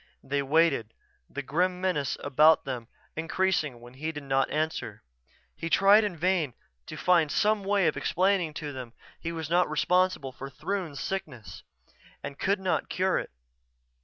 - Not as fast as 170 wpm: Yes, average, 160 wpm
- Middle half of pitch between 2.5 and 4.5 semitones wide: No, average, 4.9 semitones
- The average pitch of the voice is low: No, medium, 160 Hz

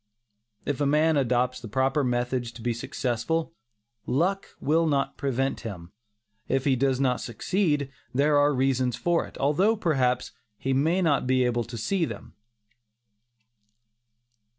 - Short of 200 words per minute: Yes, average, 145 wpm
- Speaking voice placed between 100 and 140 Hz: Yes, low, 135 Hz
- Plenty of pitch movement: No, average, 3.4 semitones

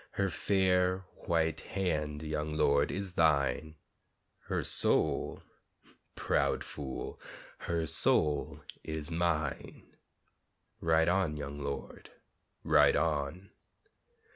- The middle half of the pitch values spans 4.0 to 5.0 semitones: No, average, 3.0 semitones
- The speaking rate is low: Yes, slow, 90 wpm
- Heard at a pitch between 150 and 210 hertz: No, very low, 80 Hz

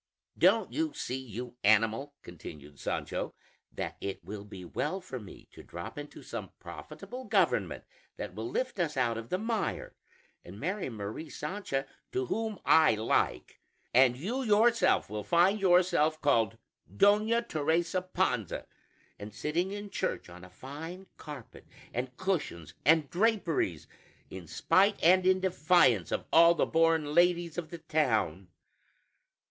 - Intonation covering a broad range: Yes, wide, 8.7 semitones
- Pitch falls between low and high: Yes, medium, 155 Hz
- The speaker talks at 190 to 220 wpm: No, average, 145 wpm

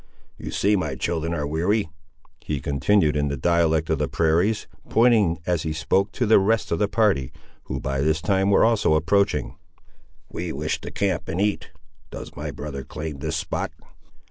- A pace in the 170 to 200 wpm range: Yes, average, 180 wpm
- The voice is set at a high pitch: No, very low, 85 Hz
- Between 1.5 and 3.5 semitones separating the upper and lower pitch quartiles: No, average, 4.7 semitones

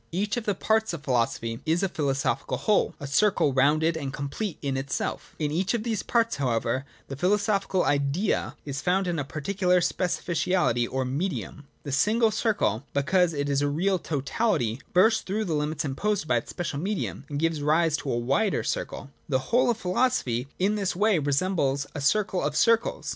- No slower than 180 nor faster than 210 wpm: Yes, average, 190 wpm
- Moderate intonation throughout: No, wide, 6.0 semitones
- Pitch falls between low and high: Yes, medium, 160 Hz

